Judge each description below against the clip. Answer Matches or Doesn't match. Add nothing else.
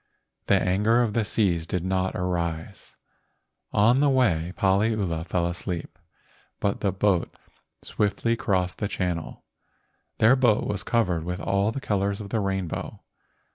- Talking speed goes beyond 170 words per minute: Doesn't match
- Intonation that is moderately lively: Matches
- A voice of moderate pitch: Doesn't match